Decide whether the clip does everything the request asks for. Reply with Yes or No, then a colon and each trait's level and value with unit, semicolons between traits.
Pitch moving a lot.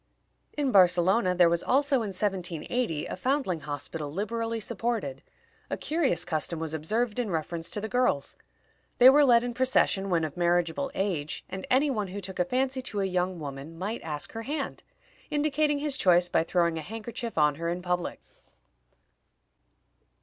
Yes: wide, 6.5 semitones